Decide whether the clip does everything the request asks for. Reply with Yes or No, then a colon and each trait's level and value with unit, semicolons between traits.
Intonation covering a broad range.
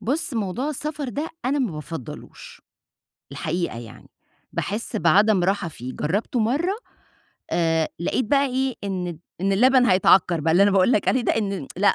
Yes: wide, 7.0 semitones